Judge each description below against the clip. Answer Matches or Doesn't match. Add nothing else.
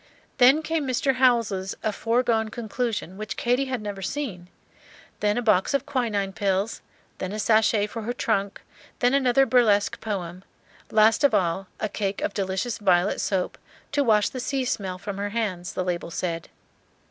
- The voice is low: Doesn't match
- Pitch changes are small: Doesn't match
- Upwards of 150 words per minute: Matches